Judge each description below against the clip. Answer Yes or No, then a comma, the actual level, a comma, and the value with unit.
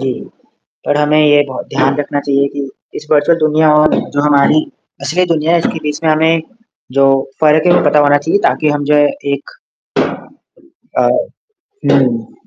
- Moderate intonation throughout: No, narrow, 1.6 semitones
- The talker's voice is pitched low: No, medium, 150 Hz